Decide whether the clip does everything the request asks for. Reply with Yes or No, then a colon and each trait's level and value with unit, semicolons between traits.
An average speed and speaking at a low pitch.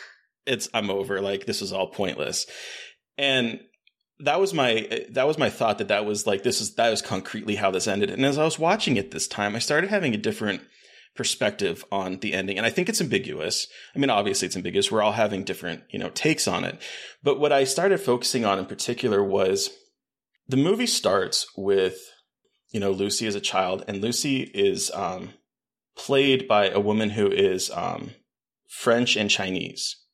Yes: average, 195 wpm; low, 115 Hz